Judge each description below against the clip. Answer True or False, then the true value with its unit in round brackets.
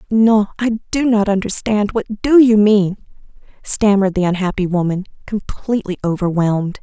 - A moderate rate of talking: False (130 wpm)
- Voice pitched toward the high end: True (205 Hz)